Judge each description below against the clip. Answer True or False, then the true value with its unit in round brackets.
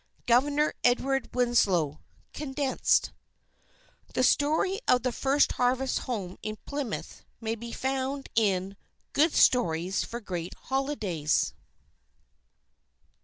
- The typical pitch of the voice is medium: False (245 Hz)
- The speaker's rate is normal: False (100 wpm)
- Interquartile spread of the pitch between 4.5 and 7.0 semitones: True (5.2 semitones)